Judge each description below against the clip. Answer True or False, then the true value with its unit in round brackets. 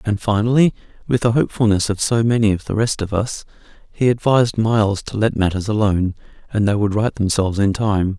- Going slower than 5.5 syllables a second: False (5.9 syllables/s)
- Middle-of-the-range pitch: False (105 Hz)